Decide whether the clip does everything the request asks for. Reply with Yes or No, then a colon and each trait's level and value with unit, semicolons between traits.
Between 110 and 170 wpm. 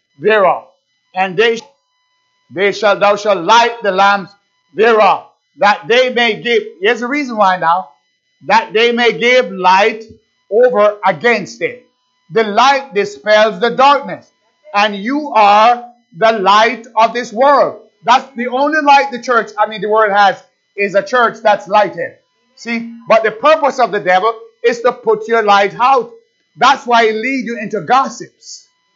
Yes: average, 160 wpm